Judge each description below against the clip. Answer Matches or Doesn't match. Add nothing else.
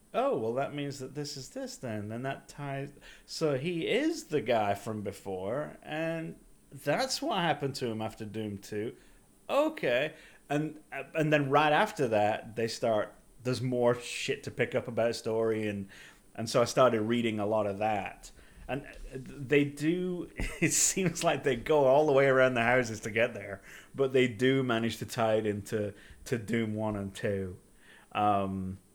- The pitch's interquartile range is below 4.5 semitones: Doesn't match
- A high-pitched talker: Doesn't match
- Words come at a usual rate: Matches